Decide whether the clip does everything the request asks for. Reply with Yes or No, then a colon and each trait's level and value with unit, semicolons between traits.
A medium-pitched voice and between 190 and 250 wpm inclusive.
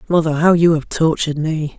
Yes: medium, 160 Hz; average, 200 wpm